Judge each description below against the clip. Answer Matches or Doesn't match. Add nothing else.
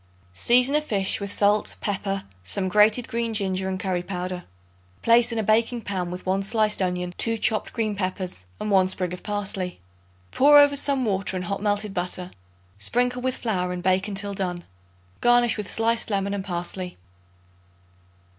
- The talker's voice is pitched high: Matches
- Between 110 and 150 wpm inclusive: Doesn't match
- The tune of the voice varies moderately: Matches